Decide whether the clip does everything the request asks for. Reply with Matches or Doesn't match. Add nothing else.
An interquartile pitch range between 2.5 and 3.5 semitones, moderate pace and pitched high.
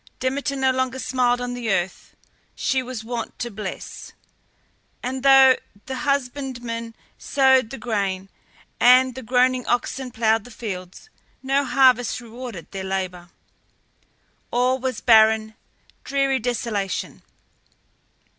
Doesn't match